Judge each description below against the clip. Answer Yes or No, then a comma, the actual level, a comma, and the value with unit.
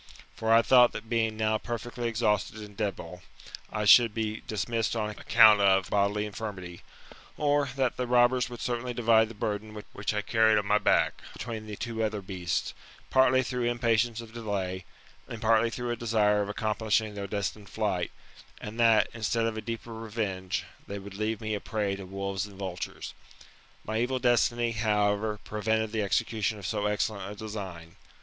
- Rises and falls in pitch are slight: Yes, narrow, 2.1 semitones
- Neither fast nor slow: Yes, average, 175 wpm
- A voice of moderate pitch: No, low, 110 Hz